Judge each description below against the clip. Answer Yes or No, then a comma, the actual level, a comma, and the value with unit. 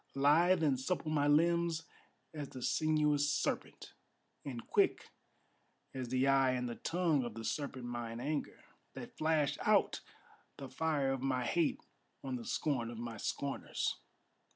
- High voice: No, medium, 140 Hz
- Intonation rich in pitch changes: No, average, 3.6 semitones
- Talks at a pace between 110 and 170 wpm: Yes, average, 150 wpm